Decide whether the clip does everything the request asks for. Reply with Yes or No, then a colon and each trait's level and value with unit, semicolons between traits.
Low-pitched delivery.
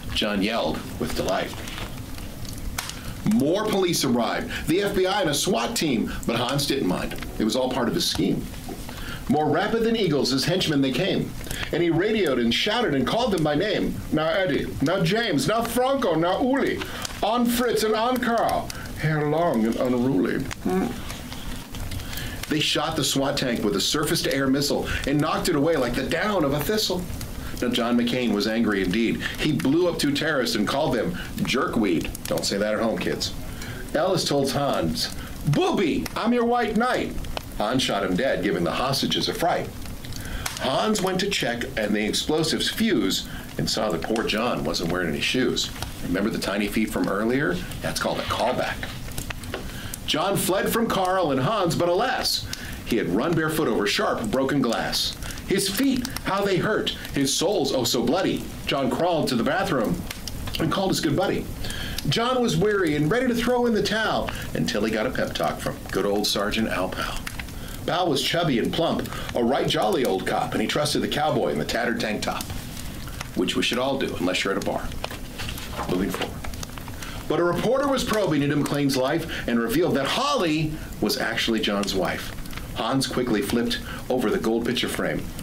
No: medium, 150 Hz